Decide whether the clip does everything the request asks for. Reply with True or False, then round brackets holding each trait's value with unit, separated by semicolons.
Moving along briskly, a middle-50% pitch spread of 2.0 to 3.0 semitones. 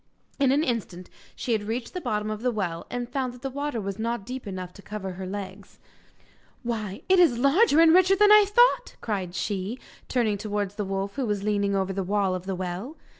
False (220 wpm; 5.1 semitones)